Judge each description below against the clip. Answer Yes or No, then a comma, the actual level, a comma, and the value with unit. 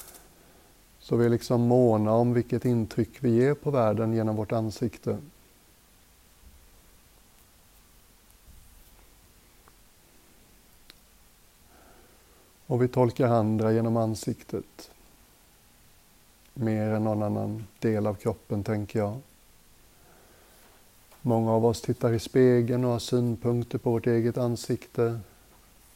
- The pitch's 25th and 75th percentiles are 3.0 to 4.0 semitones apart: No, narrow, 2.5 semitones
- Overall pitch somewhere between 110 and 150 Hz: Yes, low, 115 Hz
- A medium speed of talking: No, slow, 100 wpm